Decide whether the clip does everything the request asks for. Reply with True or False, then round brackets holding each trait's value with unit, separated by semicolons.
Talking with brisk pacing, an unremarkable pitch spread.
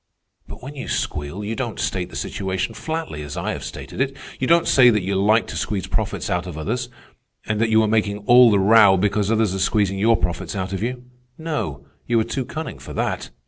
True (225 wpm; 4.2 semitones)